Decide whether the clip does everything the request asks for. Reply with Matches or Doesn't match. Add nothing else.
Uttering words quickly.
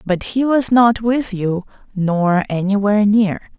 Doesn't match